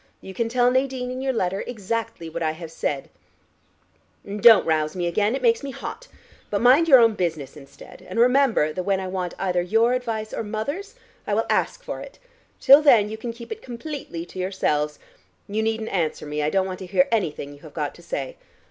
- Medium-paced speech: No, fast, 215 wpm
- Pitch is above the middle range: Yes, high, 210 Hz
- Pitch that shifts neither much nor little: No, wide, 6.1 semitones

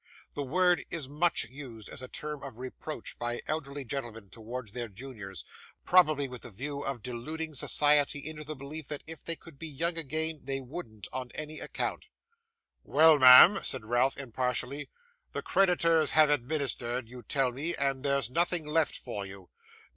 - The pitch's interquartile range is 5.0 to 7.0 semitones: No, average, 3.9 semitones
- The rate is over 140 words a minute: Yes, average, 170 wpm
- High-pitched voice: No, medium, 140 Hz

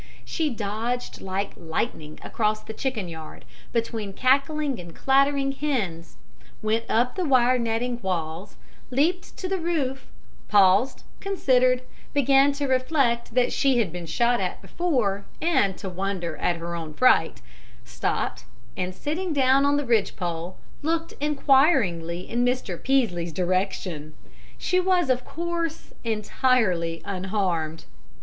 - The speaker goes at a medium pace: No, slow, 130 wpm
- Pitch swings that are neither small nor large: No, wide, 6.9 semitones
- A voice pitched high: Yes, high, 235 Hz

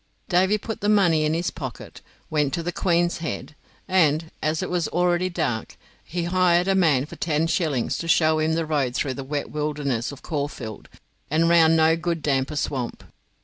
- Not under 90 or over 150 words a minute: No, average, 190 wpm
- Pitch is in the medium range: Yes, medium, 160 Hz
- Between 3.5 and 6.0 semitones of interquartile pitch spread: No, average, 3.1 semitones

